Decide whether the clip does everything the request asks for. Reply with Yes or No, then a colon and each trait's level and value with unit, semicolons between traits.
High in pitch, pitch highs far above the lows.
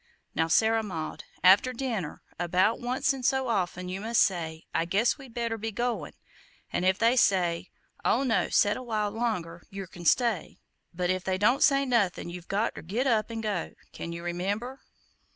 No: high, 205 Hz; average, 4.8 semitones